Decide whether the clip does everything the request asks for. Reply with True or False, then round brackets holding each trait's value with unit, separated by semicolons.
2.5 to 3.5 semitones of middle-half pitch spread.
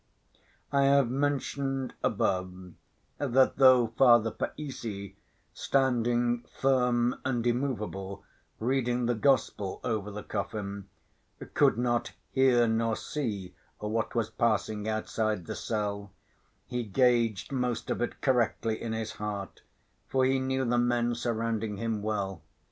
True (3.1 semitones)